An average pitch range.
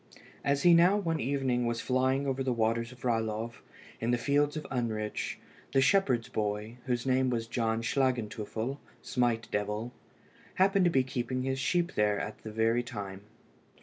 Yes: average, 3.1 semitones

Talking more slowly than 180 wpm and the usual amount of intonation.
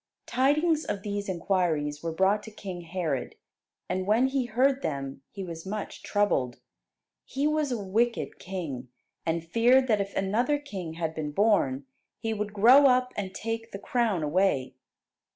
No: average, 160 wpm; wide, 6.2 semitones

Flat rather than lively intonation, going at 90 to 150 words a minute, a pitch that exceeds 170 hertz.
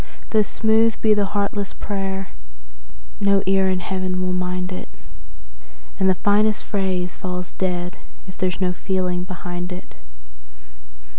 Yes: narrow, 1.7 semitones; average, 140 wpm; high, 190 Hz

